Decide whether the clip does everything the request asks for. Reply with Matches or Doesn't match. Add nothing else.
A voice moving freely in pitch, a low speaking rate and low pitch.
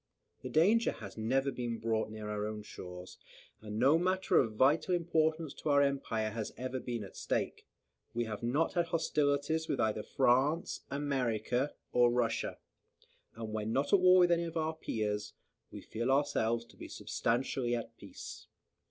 Doesn't match